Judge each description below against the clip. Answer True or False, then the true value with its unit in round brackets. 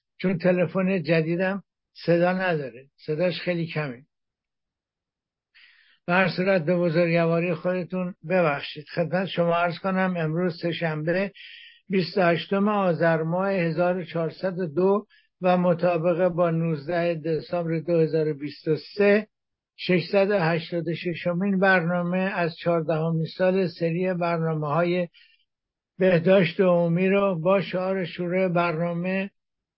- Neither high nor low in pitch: True (175 Hz)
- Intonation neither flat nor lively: False (2.0 semitones)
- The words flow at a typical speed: False (95 wpm)